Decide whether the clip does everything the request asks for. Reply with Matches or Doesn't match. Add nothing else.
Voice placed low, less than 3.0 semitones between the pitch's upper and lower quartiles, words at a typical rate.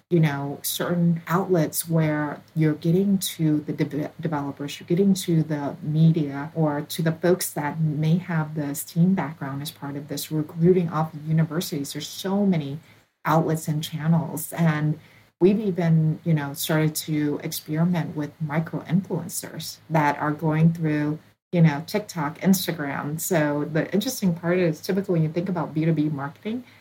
Doesn't match